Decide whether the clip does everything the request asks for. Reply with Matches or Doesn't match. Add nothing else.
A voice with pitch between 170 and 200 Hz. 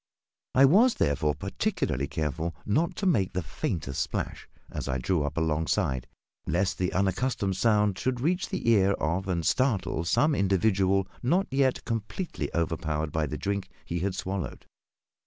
Doesn't match